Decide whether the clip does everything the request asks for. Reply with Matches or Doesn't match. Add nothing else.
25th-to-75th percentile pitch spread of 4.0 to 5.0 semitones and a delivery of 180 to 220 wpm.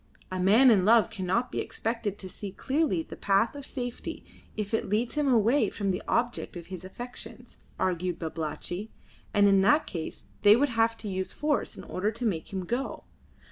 Matches